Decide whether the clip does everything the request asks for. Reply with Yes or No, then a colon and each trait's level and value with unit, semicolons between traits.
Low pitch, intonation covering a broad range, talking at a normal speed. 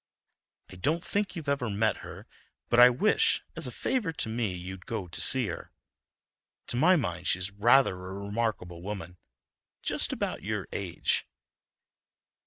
Yes: low, 105 Hz; wide, 5.8 semitones; average, 160 wpm